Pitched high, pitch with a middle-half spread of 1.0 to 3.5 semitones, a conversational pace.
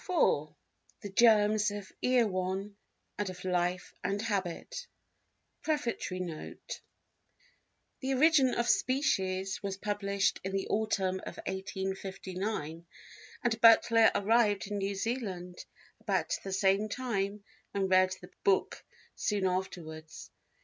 No: high, 200 Hz; average, 3.0 semitones; slow, 115 wpm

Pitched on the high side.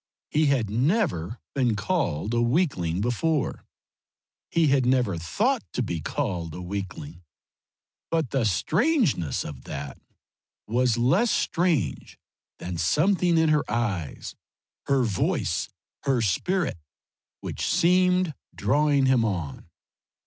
No: low, 125 Hz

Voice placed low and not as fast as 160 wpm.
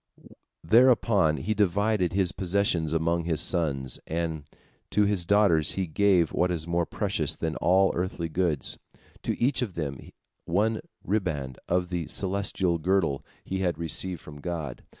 Yes: very low, 90 Hz; average, 150 wpm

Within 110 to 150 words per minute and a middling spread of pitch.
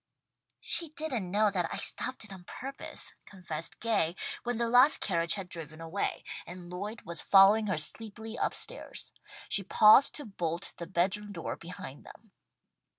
No: average, 165 wpm; average, 4.5 semitones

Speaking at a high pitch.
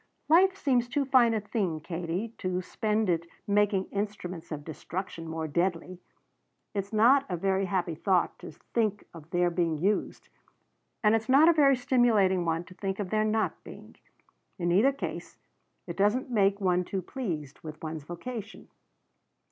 Yes: high, 195 Hz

